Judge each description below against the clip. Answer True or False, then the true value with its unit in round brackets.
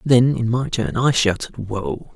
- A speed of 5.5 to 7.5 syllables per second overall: False (3.9 syllables/s)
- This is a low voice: True (120 Hz)